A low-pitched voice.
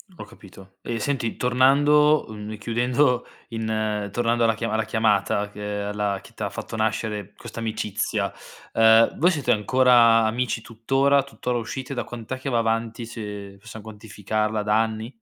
Yes: low, 115 Hz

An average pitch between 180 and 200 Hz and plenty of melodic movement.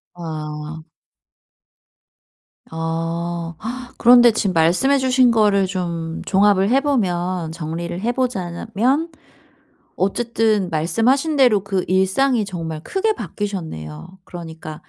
Yes: high, 190 Hz; wide, 6.1 semitones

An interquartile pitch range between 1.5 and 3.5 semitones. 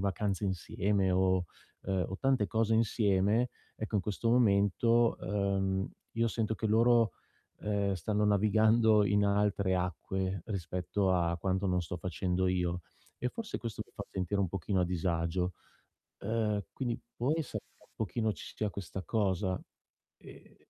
Yes: average, 2.8 semitones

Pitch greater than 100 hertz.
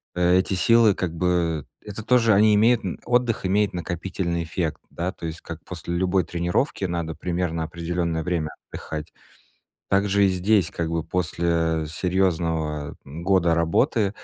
No: very low, 90 Hz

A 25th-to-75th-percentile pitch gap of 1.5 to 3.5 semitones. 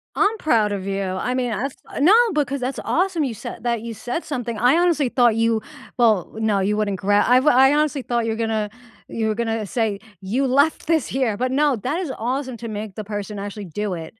No: average, 4.5 semitones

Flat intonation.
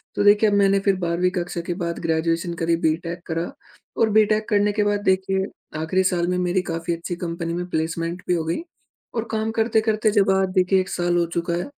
No: average, 3.2 semitones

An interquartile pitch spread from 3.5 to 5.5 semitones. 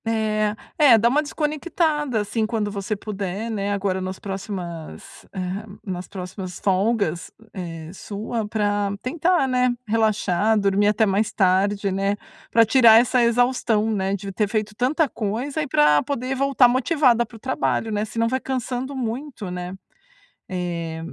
Yes: average, 4.0 semitones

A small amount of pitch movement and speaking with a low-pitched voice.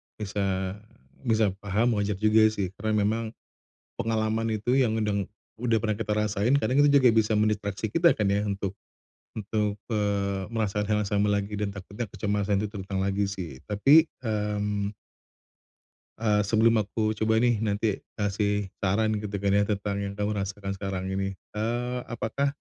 Yes: narrow, 1.7 semitones; low, 105 Hz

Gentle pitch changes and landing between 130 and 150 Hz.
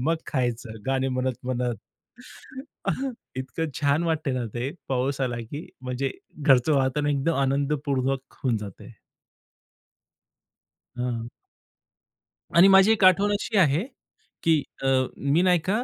No: average, 4.0 semitones; low, 135 Hz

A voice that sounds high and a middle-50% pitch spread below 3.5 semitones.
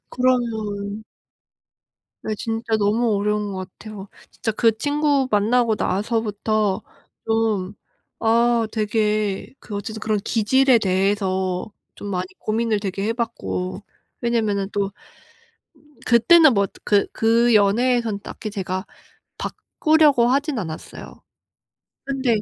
Yes: high, 215 Hz; average, 2.7 semitones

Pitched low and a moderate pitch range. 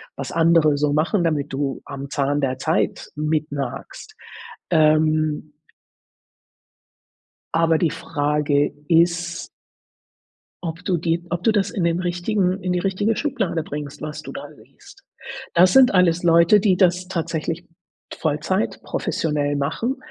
No: medium, 165 Hz; average, 3.2 semitones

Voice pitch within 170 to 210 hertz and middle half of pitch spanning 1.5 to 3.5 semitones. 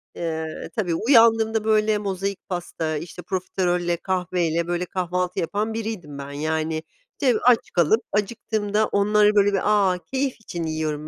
No: medium, 185 Hz; average, 4.3 semitones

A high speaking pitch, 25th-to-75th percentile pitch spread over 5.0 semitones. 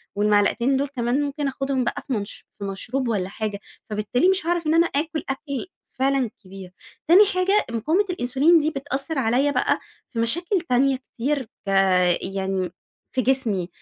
Yes: very high, 265 Hz; wide, 5.4 semitones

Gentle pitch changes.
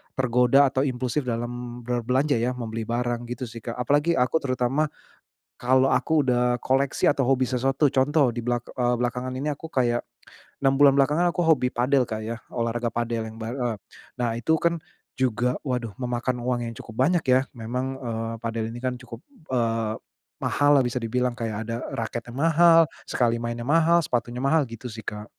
Yes: narrow, 2.3 semitones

